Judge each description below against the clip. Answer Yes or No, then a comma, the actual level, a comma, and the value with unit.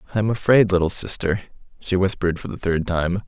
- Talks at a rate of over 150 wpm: Yes, average, 200 wpm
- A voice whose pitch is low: Yes, very low, 95 Hz